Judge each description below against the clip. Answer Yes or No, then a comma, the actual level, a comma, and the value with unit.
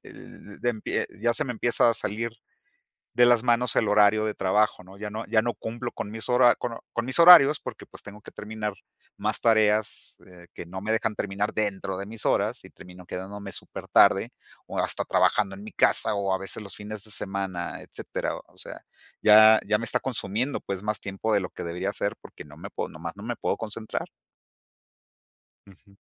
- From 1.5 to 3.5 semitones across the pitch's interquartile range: Yes, average, 2.7 semitones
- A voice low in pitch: Yes, low, 105 Hz